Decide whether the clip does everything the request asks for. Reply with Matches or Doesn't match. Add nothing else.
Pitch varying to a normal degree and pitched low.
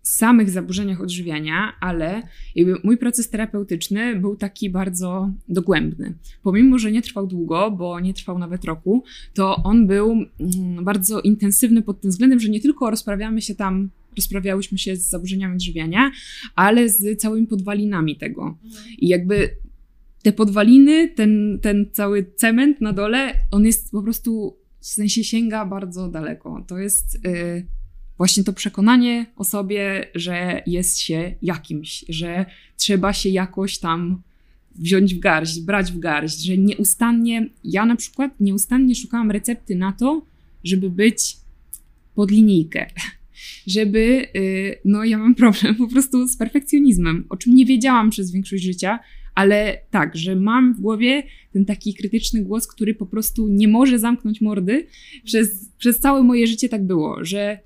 Doesn't match